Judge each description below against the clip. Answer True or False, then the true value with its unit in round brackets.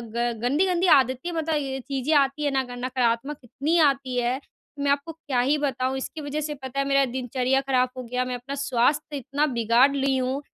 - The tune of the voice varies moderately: False (2.3 semitones)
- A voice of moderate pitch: False (270 Hz)